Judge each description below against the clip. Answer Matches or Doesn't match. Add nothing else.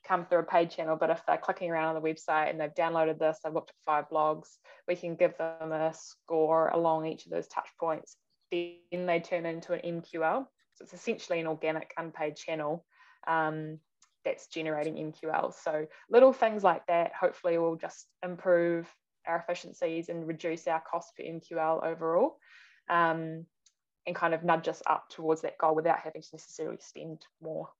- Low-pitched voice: Doesn't match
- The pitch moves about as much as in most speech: Doesn't match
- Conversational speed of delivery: Matches